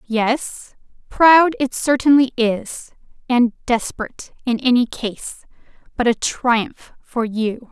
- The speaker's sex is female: Yes, female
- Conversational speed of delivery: No, slow, 115 wpm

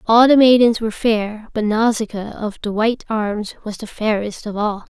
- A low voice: No, high, 220 Hz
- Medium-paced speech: Yes, average, 195 wpm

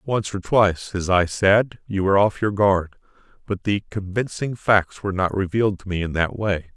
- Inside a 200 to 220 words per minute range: Yes, fast, 205 wpm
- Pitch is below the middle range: Yes, low, 100 Hz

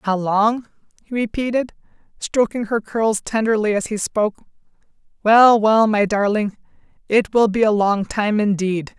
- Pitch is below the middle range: No, high, 215 Hz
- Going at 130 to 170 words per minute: Yes, average, 145 wpm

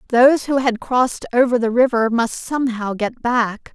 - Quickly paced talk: No, average, 175 wpm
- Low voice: No, high, 240 Hz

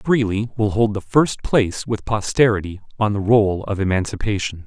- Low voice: Yes, low, 105 Hz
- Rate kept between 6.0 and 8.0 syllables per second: No, 5.1 syllables/s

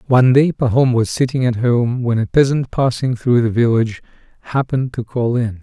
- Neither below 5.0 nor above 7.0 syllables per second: Yes, 5.4 syllables/s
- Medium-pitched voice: No, low, 120 Hz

